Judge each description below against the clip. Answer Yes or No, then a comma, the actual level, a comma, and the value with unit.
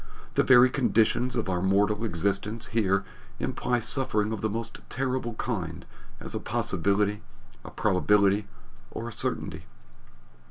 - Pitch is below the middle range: Yes, low, 105 Hz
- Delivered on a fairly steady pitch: No, average, 3.1 semitones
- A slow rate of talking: Yes, slow, 130 wpm